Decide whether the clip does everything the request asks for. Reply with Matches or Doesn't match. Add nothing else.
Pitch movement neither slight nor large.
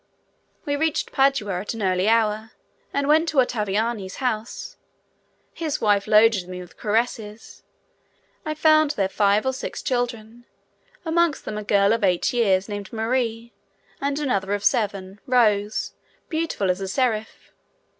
Matches